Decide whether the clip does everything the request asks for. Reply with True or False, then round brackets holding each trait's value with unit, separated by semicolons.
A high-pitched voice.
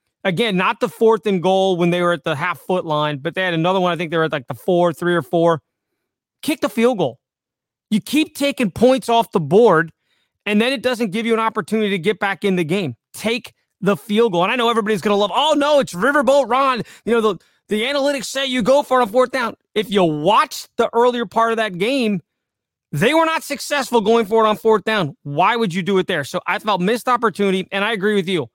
True (215 Hz)